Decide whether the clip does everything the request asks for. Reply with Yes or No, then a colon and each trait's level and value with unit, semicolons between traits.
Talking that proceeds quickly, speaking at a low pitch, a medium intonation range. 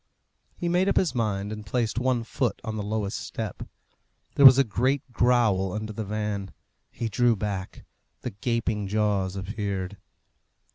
No: average, 155 wpm; low, 110 Hz; average, 3.2 semitones